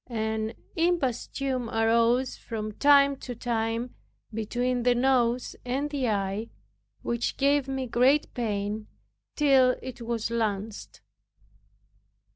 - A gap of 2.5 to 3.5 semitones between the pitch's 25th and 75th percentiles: Yes, average, 2.8 semitones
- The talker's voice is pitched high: Yes, high, 240 Hz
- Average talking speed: No, slow, 105 wpm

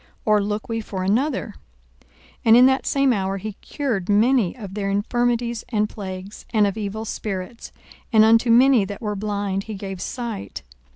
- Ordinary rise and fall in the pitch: Yes, average, 3.0 semitones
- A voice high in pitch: Yes, high, 215 Hz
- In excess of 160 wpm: Yes, average, 175 wpm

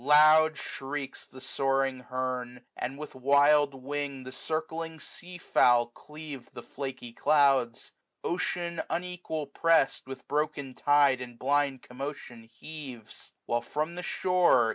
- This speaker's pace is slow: Yes, slow, 125 wpm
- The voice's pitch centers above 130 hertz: Yes, medium, 140 Hz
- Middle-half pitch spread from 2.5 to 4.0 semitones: Yes, average, 3.1 semitones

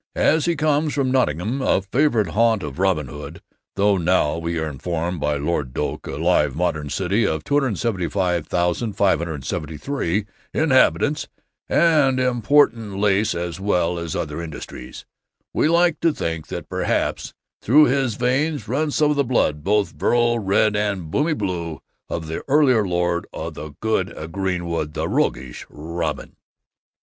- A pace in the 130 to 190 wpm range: Yes, average, 145 wpm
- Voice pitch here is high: No, very low, 95 Hz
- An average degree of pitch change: No, wide, 7.5 semitones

